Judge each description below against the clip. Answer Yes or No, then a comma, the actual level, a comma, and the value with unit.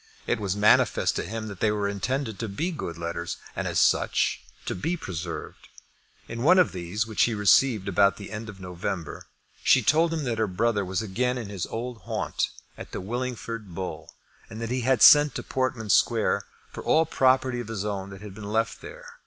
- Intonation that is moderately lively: Yes, average, 4.2 semitones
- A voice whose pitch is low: Yes, low, 110 Hz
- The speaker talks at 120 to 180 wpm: No, fast, 205 wpm